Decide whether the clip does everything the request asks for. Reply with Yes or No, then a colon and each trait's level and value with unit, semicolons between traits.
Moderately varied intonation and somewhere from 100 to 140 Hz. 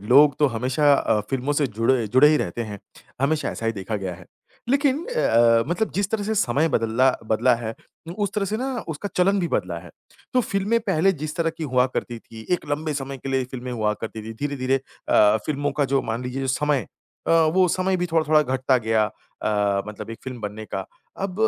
No: wide, 6.4 semitones; low, 135 Hz